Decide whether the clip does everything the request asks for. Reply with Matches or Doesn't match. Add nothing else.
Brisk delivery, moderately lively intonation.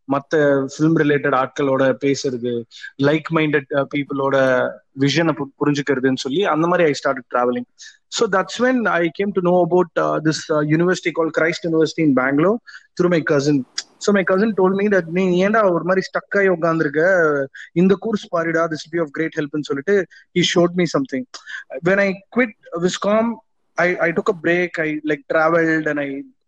Matches